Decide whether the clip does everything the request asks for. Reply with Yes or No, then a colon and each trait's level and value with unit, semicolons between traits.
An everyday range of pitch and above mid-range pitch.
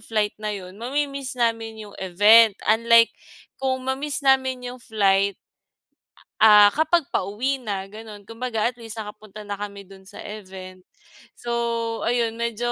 Yes: average, 3.2 semitones; high, 220 Hz